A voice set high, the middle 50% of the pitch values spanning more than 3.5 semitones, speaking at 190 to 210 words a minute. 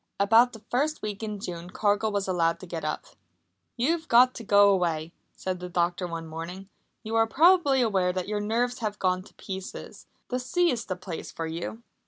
Yes: high, 200 Hz; average, 4.6 semitones; average, 200 wpm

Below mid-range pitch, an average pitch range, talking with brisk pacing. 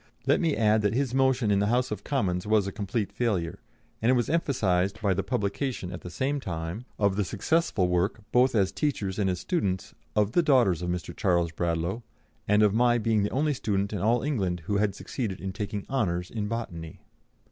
Yes: low, 105 Hz; average, 4.6 semitones; fast, 210 wpm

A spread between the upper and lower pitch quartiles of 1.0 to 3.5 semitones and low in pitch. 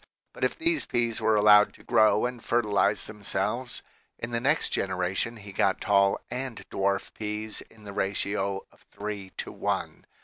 Yes: average, 3.0 semitones; low, 105 Hz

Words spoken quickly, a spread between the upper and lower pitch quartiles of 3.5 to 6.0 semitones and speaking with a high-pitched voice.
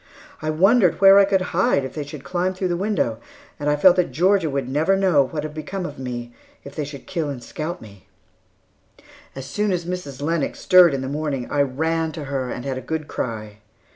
No: fast, 220 wpm; average, 4.9 semitones; medium, 155 Hz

